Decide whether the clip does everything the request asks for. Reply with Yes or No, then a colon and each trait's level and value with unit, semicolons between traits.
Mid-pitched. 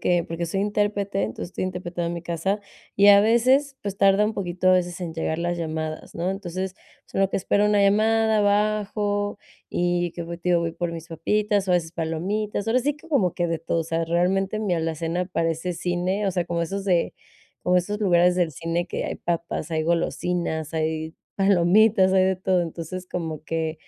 Yes: medium, 180 Hz